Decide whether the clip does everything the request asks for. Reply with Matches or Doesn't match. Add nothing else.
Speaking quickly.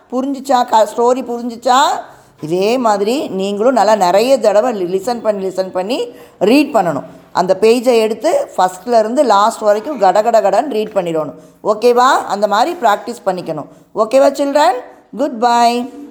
Matches